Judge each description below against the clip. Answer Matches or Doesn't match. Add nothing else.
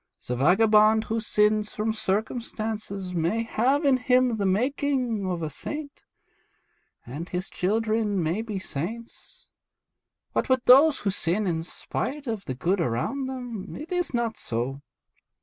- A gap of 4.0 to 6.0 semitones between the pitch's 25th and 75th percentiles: Matches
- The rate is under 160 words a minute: Matches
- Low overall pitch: Doesn't match